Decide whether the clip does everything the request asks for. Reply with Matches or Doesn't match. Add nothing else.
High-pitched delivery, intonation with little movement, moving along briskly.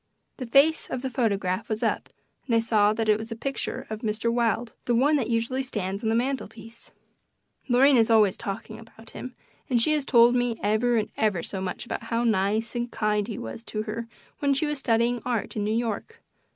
Matches